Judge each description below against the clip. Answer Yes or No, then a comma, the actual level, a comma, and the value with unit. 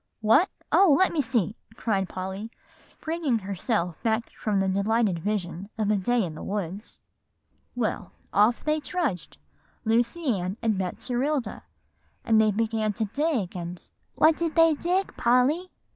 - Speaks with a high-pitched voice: Yes, high, 220 Hz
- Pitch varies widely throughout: Yes, wide, 6.2 semitones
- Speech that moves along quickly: No, average, 145 wpm